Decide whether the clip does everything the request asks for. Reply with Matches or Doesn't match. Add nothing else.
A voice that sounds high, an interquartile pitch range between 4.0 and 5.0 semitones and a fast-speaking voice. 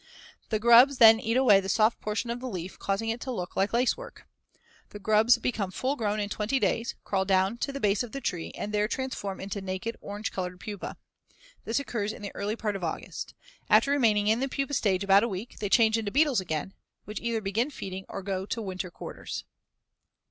Doesn't match